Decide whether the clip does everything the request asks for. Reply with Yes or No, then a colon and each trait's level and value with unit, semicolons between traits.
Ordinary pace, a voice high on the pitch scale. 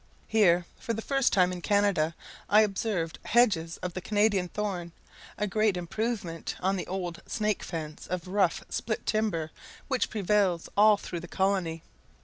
Yes: average, 155 wpm; high, 195 Hz